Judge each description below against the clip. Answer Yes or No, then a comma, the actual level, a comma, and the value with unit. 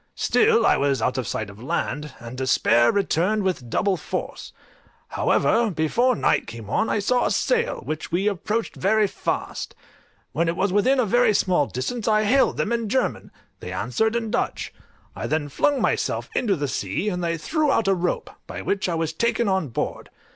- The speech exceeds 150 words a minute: Yes, average, 190 wpm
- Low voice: No, high, 190 Hz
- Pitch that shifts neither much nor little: No, wide, 7.5 semitones